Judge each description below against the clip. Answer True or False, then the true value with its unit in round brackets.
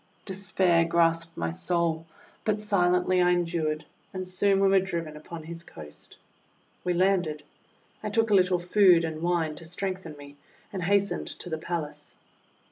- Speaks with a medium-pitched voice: True (175 Hz)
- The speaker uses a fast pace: False (160 wpm)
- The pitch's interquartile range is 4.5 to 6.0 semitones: False (2.6 semitones)